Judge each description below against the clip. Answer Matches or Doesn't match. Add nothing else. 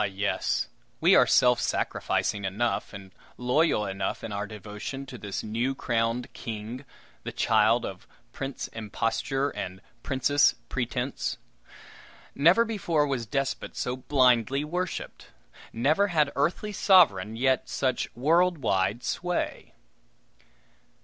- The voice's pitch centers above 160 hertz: Doesn't match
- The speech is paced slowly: Matches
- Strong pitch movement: Doesn't match